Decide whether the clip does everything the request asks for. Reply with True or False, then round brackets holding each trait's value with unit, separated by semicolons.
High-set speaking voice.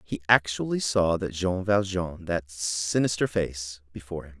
False (90 Hz)